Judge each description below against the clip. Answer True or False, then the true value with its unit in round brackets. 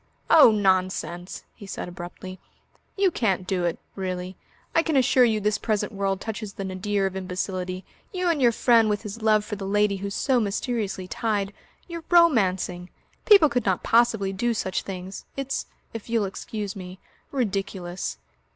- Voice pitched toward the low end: False (200 Hz)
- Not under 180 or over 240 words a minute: False (165 wpm)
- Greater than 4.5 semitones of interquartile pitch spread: False (3.6 semitones)